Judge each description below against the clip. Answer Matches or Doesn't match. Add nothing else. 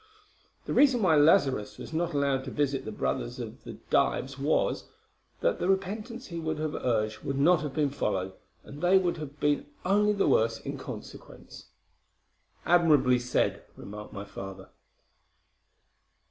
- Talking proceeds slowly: Doesn't match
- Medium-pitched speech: Matches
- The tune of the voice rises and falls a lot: Matches